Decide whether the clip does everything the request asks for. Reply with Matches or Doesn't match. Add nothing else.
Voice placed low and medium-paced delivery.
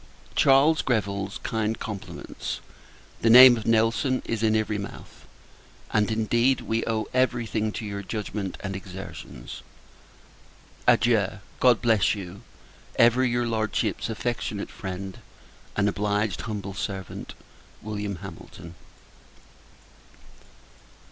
Doesn't match